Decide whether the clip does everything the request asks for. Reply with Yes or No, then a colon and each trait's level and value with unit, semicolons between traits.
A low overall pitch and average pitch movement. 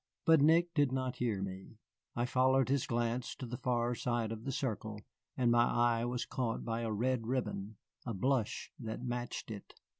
No: low, 120 Hz; narrow, 2.2 semitones